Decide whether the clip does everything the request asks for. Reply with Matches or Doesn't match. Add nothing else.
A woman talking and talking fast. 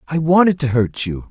Doesn't match